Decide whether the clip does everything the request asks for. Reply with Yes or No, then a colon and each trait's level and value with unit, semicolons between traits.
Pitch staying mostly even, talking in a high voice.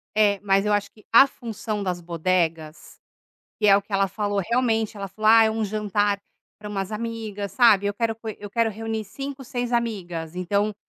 Yes: narrow, 2.3 semitones; high, 210 Hz